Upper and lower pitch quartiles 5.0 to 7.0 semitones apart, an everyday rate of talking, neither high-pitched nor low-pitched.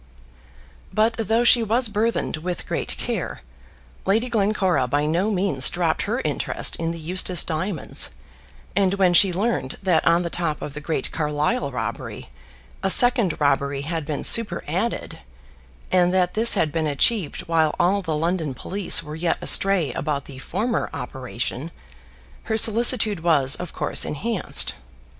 Yes: average, 5.3 semitones; average, 150 wpm; medium, 175 Hz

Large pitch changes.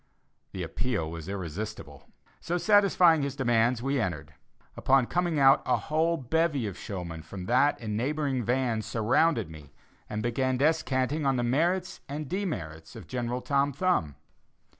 Yes: wide, 6.4 semitones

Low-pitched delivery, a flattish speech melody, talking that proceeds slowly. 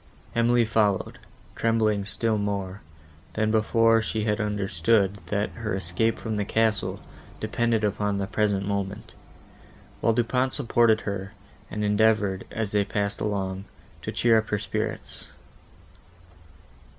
Yes: low, 105 Hz; narrow, 2.0 semitones; slow, 125 wpm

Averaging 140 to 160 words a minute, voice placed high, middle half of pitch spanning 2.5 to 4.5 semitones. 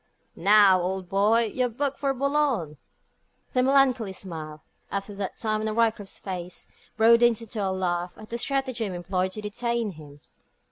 Yes: average, 155 wpm; high, 215 Hz; average, 4.2 semitones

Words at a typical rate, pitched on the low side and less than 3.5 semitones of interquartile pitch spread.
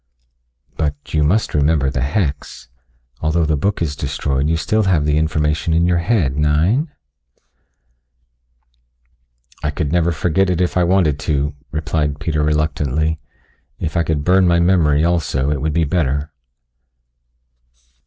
Yes: average, 145 wpm; very low, 80 Hz; average, 2.7 semitones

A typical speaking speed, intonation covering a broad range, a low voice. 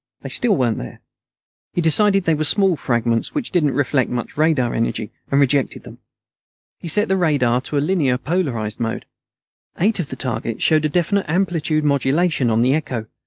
No: average, 180 wpm; wide, 6.0 semitones; medium, 145 Hz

